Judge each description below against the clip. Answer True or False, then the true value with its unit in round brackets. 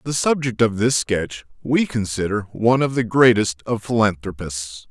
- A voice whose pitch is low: True (115 Hz)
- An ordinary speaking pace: True (160 wpm)